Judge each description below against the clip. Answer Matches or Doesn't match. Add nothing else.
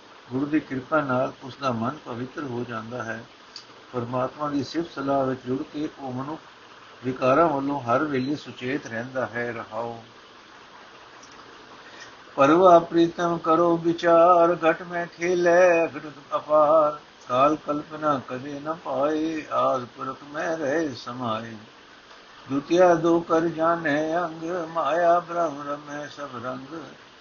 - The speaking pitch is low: Doesn't match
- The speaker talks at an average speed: Matches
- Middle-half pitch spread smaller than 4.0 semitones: Doesn't match